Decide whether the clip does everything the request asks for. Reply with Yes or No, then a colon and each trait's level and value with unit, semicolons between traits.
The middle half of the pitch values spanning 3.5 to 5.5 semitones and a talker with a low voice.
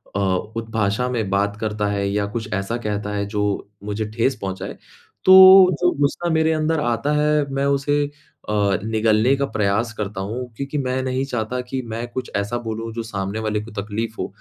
Yes: average, 4.4 semitones; low, 115 Hz